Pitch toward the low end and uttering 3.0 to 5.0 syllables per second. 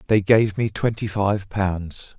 Yes: low, 100 Hz; 3.6 syllables/s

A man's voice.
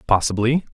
Yes: male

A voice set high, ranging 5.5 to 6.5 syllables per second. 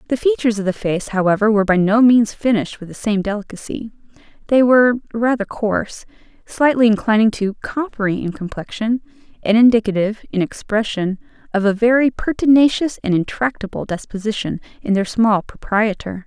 Yes: high, 220 Hz; 5.6 syllables/s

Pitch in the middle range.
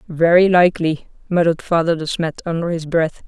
Yes: medium, 165 Hz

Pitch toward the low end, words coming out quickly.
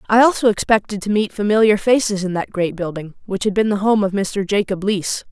No: high, 205 Hz; fast, 225 wpm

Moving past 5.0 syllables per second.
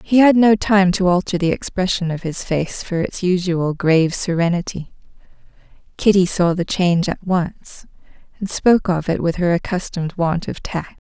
No: 4.9 syllables/s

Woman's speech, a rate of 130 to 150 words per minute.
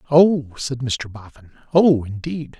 No: male; average, 140 wpm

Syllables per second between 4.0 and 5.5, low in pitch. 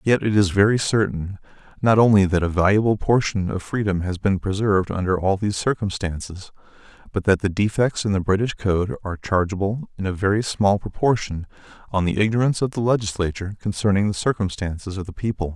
No: 6.0 syllables/s; low, 100 Hz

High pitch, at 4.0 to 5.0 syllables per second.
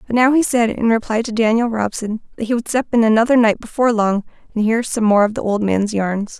No: high, 225 Hz; 5.9 syllables/s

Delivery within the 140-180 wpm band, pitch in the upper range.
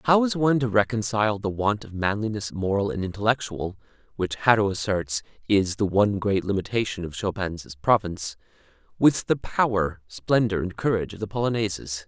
No: average, 160 wpm; low, 105 Hz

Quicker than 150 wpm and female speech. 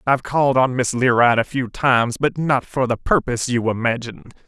No: average, 200 wpm; male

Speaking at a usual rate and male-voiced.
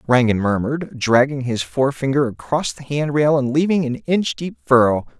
Yes: average, 175 wpm; male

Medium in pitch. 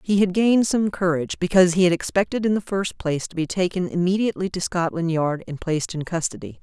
Yes: medium, 180 Hz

